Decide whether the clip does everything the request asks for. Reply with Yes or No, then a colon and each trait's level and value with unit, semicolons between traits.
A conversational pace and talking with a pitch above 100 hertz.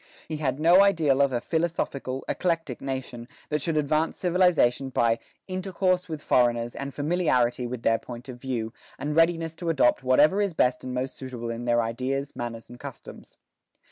Yes: average, 170 wpm; low, 135 Hz